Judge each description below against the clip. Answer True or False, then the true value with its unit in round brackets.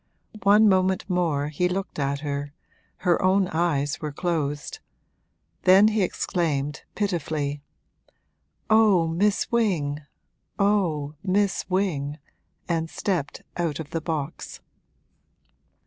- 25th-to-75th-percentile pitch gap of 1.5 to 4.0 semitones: False (4.6 semitones)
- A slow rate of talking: True (105 wpm)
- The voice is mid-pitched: True (170 Hz)